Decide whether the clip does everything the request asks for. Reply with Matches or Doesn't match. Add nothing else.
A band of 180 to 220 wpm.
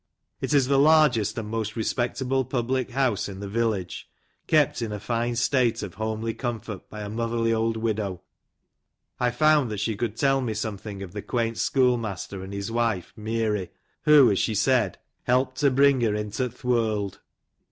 Matches